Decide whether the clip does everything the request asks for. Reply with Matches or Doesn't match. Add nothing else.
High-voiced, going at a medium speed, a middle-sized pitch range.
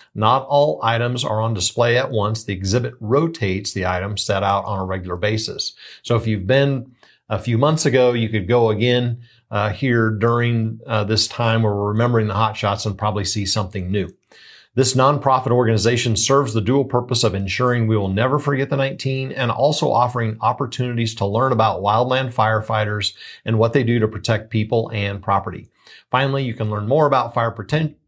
Doesn't match